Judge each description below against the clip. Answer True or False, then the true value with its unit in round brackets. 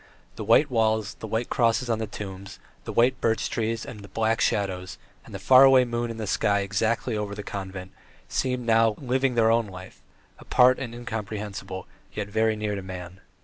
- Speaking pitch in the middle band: False (110 Hz)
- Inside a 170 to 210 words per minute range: True (190 wpm)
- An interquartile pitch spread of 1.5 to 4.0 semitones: True (2.7 semitones)